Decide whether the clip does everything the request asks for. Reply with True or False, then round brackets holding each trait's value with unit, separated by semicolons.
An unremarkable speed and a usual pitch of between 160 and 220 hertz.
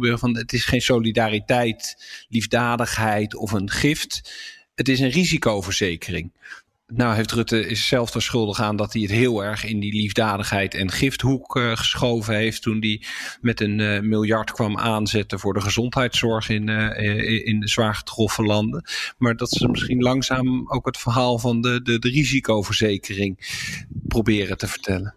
False (160 wpm; 115 Hz)